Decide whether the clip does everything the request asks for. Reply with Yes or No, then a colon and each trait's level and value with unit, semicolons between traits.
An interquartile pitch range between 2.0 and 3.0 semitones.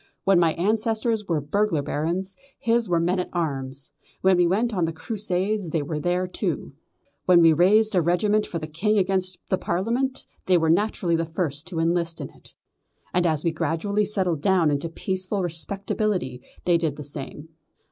No: average, 3.5 semitones